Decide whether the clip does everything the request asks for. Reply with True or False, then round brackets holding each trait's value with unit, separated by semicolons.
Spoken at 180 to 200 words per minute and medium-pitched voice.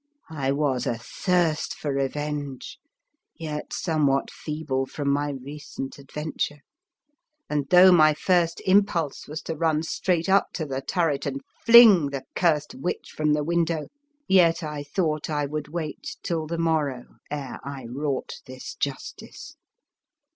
False (140 wpm; 150 Hz)